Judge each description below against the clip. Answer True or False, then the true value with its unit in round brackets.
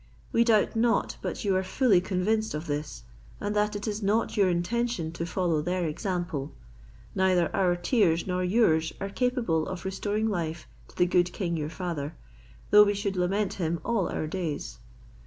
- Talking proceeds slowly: False (175 wpm)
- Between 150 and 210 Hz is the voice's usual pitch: True (185 Hz)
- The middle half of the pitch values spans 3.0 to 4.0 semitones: True (3.7 semitones)